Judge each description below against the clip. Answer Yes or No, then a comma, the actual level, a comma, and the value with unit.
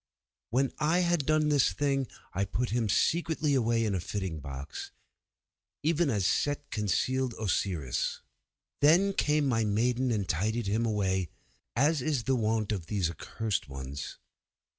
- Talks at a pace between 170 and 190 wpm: No, average, 145 wpm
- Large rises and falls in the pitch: Yes, wide, 6.4 semitones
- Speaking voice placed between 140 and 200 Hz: No, low, 115 Hz